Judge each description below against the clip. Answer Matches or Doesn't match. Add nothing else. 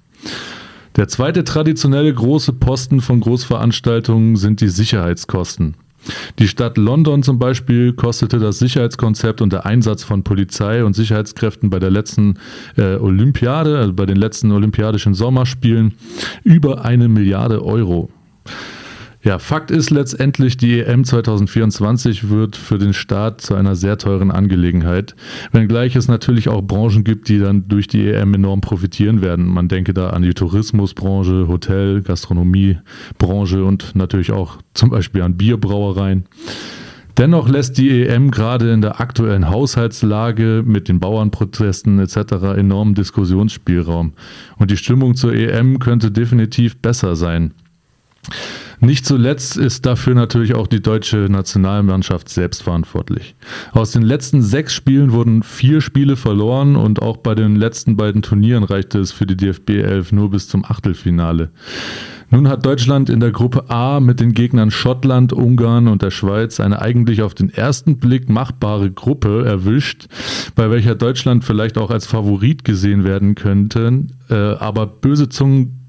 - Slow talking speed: Doesn't match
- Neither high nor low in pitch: Doesn't match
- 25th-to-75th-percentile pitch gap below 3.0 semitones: Doesn't match